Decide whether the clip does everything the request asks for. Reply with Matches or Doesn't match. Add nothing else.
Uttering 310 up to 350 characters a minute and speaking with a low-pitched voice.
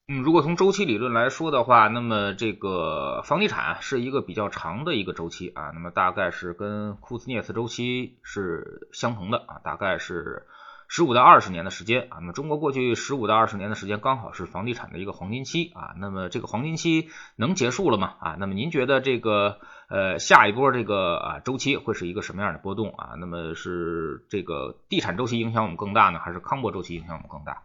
Matches